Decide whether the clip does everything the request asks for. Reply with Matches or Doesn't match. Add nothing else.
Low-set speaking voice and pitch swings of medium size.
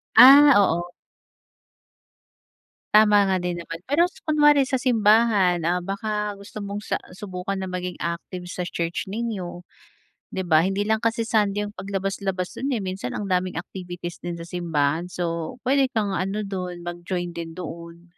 Doesn't match